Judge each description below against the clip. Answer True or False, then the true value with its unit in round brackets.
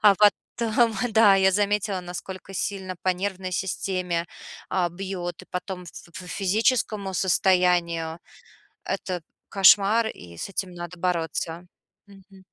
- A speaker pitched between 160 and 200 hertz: True (190 Hz)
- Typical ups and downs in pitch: False (2.0 semitones)